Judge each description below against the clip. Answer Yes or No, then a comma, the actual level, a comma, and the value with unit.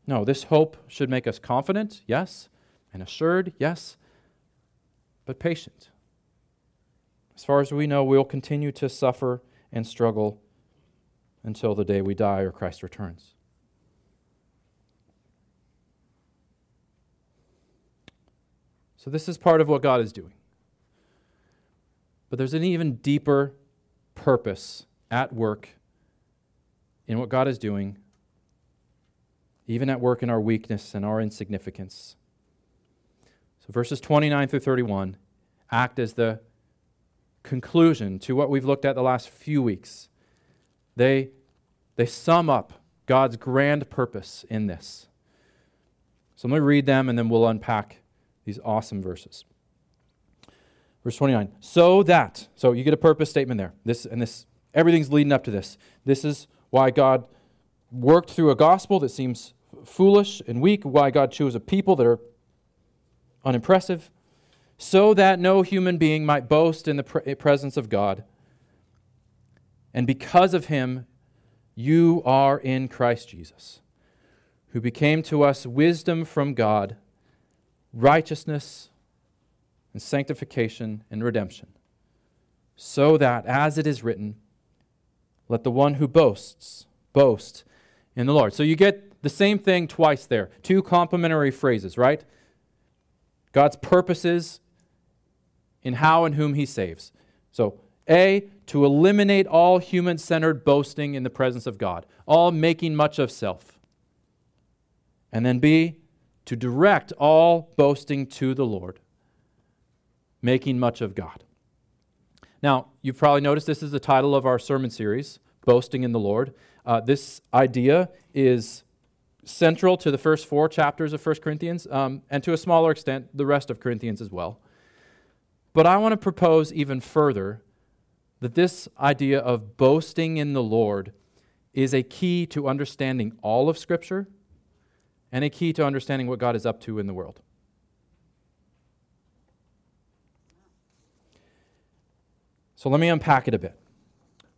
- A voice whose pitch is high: No, low, 135 Hz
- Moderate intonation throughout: Yes, average, 5.0 semitones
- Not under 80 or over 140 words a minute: Yes, slow, 135 wpm